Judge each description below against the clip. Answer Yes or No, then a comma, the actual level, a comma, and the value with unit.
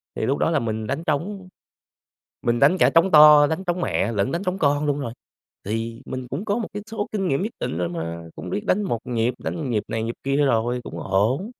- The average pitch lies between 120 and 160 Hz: Yes, medium, 140 Hz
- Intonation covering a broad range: Yes, wide, 7.7 semitones